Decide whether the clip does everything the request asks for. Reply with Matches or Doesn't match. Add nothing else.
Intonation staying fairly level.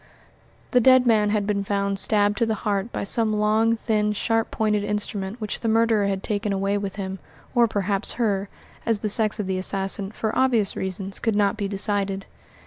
Matches